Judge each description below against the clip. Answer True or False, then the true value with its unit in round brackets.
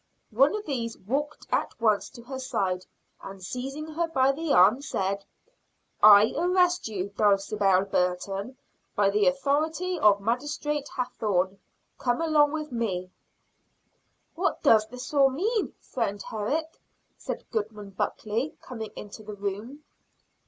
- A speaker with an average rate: False (130 wpm)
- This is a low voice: False (230 Hz)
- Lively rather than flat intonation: True (6.5 semitones)